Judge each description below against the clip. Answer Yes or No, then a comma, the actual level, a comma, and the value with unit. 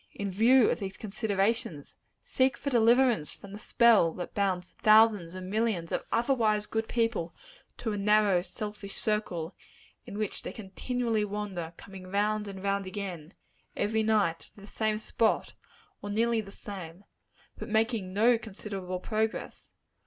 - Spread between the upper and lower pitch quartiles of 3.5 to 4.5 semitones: No, average, 2.7 semitones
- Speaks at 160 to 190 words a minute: No, average, 150 wpm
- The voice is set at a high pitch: Yes, high, 210 Hz